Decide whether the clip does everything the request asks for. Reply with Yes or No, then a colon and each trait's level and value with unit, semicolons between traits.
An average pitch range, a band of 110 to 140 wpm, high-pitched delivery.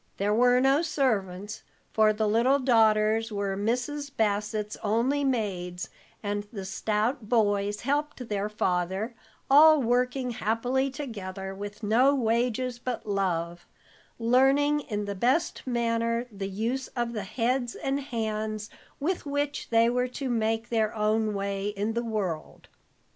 Yes: average, 3.4 semitones; slow, 135 wpm; high, 225 Hz